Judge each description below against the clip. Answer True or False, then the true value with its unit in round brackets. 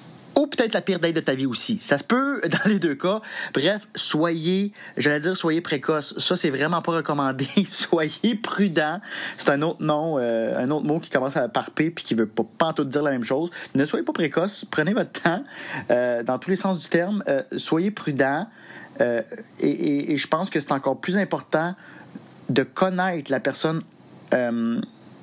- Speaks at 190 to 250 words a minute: True (200 wpm)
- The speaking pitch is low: False (170 Hz)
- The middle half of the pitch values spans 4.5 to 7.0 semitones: True (4.9 semitones)